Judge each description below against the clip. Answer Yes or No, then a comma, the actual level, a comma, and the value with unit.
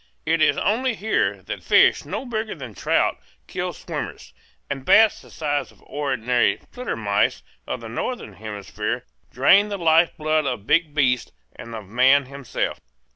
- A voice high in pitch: No, medium, 140 Hz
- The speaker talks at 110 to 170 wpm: Yes, average, 160 wpm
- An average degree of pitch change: No, wide, 6.1 semitones